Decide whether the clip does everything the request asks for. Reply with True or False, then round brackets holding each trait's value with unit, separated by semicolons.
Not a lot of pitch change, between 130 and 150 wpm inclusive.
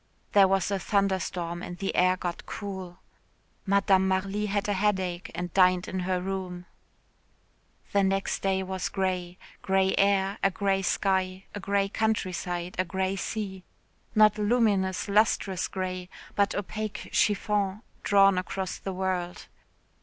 True (1.4 semitones; 140 wpm)